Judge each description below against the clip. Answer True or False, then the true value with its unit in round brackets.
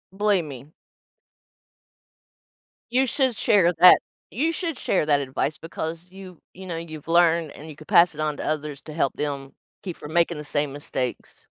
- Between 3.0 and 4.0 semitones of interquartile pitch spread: True (3.6 semitones)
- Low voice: False (165 Hz)